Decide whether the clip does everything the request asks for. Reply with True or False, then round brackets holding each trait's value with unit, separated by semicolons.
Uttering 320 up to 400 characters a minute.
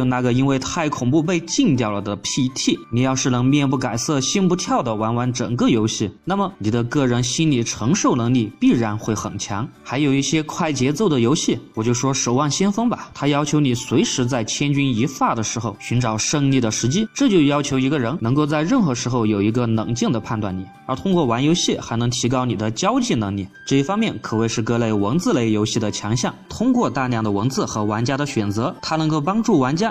True (330 characters per minute)